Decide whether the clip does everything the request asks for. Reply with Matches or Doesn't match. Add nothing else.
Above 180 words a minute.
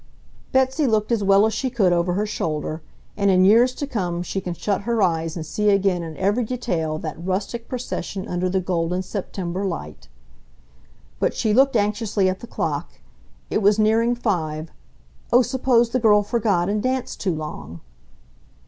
Doesn't match